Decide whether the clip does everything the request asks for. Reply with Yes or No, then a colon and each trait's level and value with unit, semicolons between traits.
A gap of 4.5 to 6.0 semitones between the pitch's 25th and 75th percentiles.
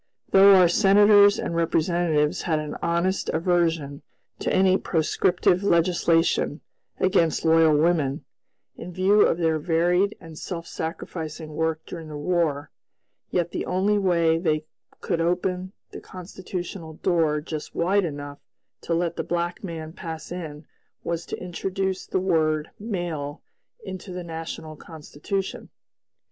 No: narrow, 2.6 semitones